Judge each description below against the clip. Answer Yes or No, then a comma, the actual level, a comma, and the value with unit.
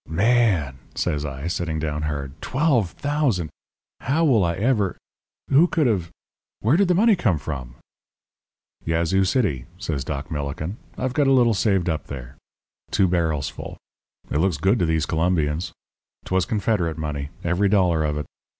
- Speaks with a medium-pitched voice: No, very low, 85 Hz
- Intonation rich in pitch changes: Yes, wide, 6.9 semitones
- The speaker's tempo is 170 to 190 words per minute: No, average, 160 wpm